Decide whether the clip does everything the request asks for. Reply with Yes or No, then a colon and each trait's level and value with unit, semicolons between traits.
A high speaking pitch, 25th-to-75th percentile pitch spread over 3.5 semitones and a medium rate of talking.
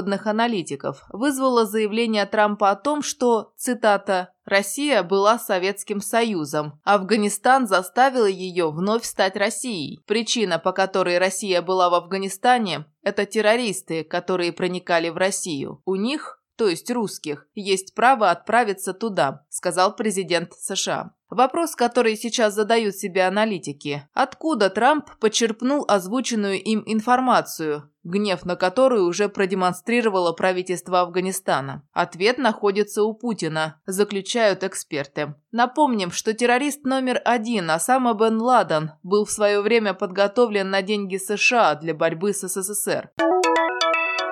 Yes: high, 205 Hz; average, 4.0 semitones; average, 120 wpm